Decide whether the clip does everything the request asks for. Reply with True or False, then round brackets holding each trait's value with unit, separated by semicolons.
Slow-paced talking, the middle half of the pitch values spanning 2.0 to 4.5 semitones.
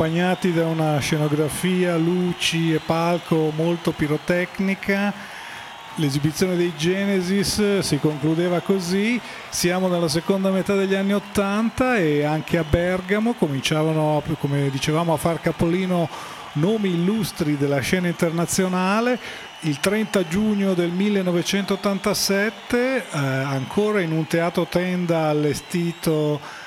True (110 wpm; 3.7 semitones)